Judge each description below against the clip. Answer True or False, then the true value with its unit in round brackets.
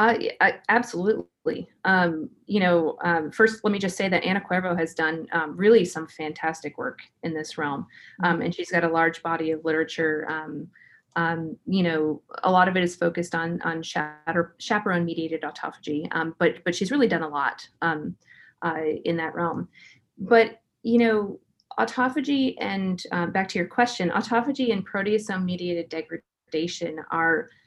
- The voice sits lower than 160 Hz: False (170 Hz)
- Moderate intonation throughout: True (3.9 semitones)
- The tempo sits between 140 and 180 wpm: True (165 wpm)